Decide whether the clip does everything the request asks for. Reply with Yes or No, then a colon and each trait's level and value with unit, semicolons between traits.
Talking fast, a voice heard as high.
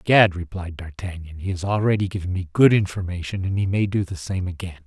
No: fast, 210 wpm; very low, 95 Hz